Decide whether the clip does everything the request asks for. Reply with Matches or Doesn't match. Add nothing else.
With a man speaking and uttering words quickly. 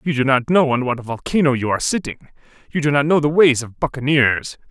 Matches